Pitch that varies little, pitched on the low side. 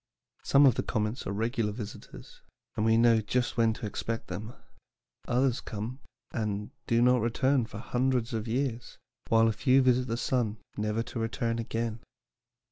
Yes: narrow, 2.2 semitones; low, 115 Hz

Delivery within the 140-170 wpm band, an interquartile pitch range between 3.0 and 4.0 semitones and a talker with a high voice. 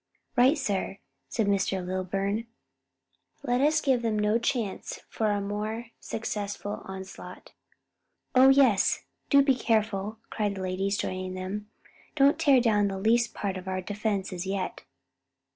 Yes: average, 145 wpm; average, 3.5 semitones; high, 210 Hz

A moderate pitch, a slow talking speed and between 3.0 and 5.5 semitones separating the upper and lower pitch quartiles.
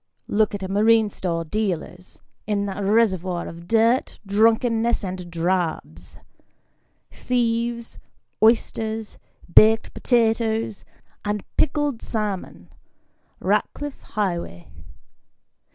No: high, 215 Hz; slow, 90 wpm; average, 3.5 semitones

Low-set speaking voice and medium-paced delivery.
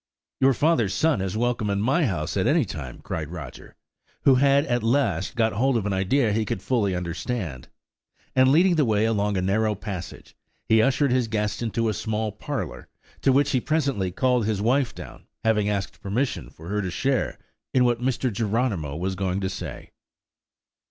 Yes: low, 110 Hz; average, 185 wpm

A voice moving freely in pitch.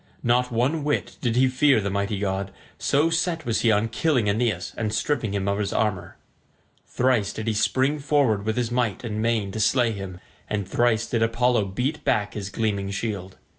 No: average, 3.7 semitones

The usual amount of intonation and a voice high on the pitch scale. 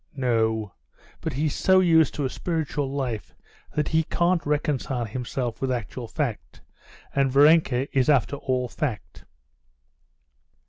No: average, 3.7 semitones; low, 135 Hz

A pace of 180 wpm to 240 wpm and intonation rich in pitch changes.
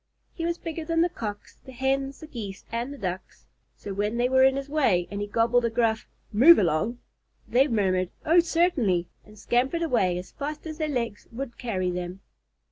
Yes: average, 200 wpm; wide, 5.8 semitones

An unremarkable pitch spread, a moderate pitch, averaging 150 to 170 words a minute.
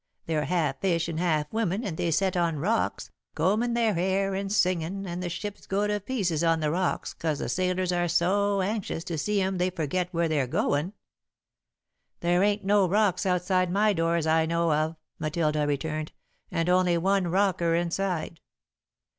No: average, 3.0 semitones; medium, 180 Hz; average, 180 wpm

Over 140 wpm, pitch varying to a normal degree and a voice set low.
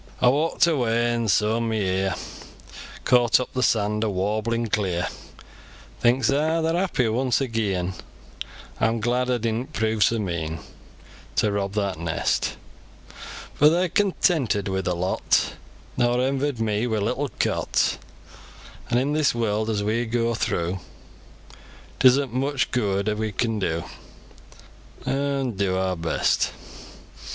No: slow, 135 wpm; average, 4.0 semitones; low, 115 Hz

